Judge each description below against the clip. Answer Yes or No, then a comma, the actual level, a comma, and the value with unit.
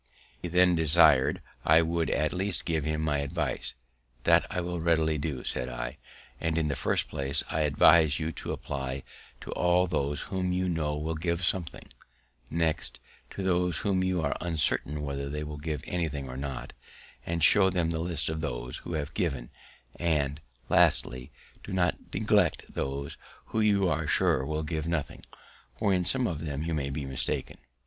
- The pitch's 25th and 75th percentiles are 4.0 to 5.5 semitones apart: No, average, 3.3 semitones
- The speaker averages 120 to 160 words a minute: No, average, 180 wpm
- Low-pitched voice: Yes, very low, 80 Hz